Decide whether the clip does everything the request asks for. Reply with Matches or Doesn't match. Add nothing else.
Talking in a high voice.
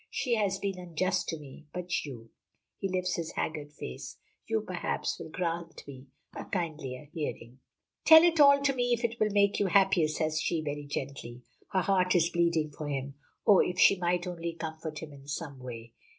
Doesn't match